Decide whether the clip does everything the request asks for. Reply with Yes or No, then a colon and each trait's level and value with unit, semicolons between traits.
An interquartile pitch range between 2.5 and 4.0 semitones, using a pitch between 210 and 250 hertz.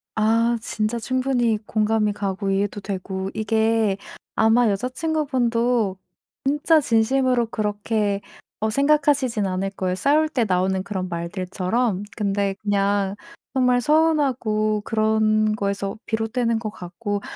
Yes: average, 3.5 semitones; high, 215 Hz